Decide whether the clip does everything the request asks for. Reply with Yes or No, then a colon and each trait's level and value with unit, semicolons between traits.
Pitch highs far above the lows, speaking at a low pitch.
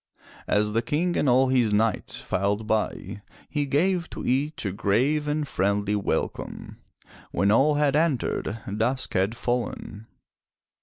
Yes: wide, 6.0 semitones; low, 120 Hz